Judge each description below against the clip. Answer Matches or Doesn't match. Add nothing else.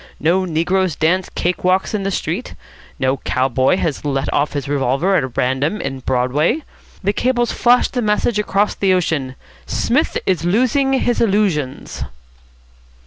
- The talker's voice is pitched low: Doesn't match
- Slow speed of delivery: Doesn't match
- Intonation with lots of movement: Matches